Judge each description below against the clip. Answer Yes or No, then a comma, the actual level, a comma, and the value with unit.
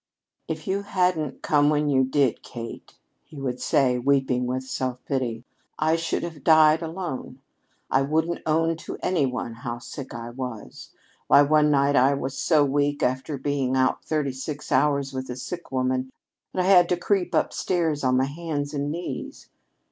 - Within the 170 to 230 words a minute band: Yes, average, 175 wpm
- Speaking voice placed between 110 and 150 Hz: Yes, medium, 140 Hz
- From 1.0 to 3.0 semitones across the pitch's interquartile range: No, average, 3.4 semitones